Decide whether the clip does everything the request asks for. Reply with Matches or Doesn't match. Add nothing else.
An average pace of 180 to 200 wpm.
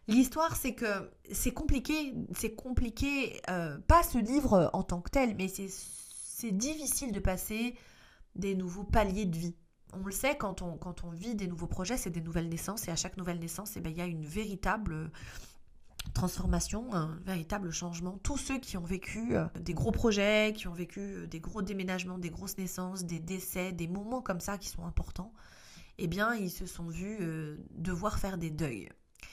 Matches